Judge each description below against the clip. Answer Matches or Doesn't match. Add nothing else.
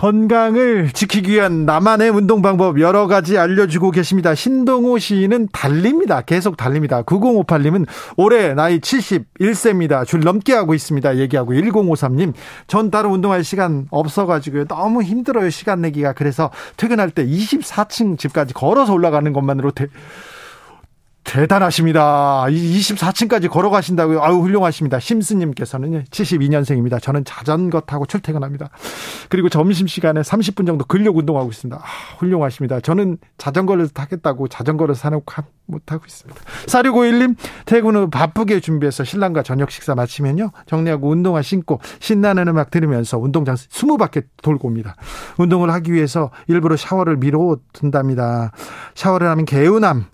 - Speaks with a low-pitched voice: Doesn't match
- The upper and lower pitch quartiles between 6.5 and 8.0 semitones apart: Doesn't match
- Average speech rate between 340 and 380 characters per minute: Matches